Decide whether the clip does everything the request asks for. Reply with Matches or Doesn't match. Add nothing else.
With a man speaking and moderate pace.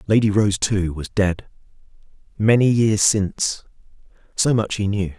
Doesn't match